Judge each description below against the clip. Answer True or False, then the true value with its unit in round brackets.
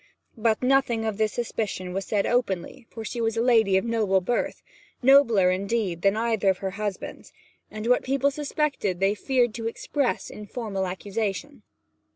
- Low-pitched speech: False (220 Hz)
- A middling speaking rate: True (170 wpm)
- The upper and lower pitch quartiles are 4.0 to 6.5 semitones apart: False (3.6 semitones)